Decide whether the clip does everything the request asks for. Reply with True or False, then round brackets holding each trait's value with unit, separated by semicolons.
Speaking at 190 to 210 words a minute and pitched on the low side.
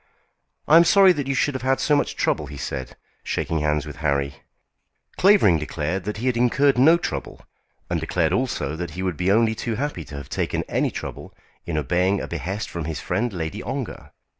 True (205 wpm; 95 Hz)